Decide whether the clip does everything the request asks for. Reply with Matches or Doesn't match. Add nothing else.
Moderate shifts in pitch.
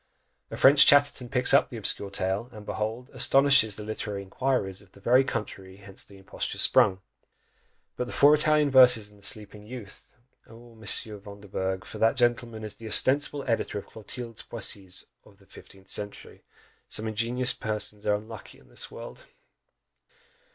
Matches